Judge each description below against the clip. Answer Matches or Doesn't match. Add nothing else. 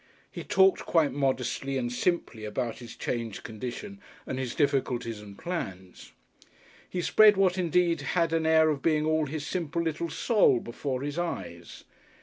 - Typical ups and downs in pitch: Doesn't match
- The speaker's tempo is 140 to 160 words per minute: Matches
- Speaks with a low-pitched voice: Doesn't match